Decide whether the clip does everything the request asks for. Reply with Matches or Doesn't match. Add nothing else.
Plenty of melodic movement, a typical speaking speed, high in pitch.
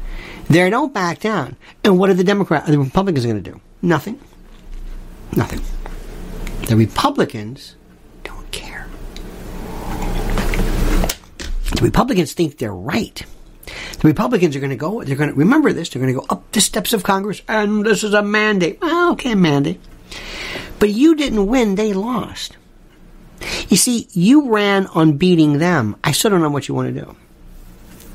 Doesn't match